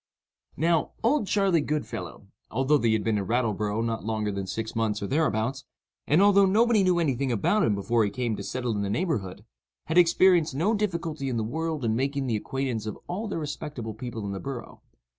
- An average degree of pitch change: No, wide, 7.0 semitones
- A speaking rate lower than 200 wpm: No, fast, 205 wpm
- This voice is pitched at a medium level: No, low, 130 Hz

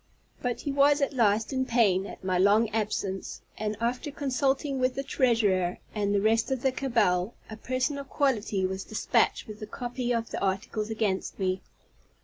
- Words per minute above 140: Yes, average, 180 wpm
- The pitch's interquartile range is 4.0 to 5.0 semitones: Yes, average, 4.3 semitones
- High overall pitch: Yes, high, 225 Hz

